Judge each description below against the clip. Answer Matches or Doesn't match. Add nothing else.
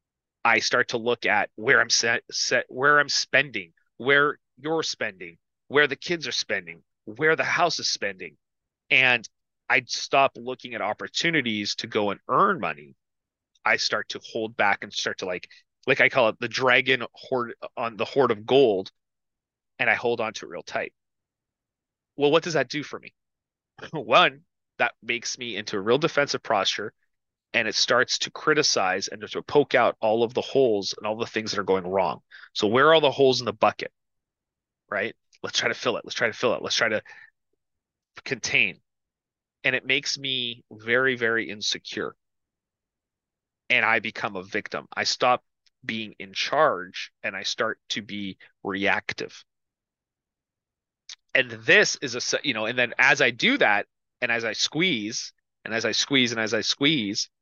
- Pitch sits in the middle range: Doesn't match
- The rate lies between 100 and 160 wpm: Doesn't match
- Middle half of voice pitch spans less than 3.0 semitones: Doesn't match